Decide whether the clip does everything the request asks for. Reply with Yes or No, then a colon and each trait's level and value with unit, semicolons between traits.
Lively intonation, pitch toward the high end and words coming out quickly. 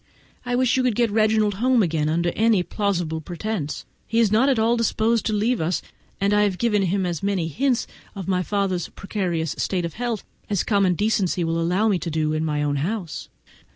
No: average, 4.5 semitones; high, 200 Hz; fast, 210 wpm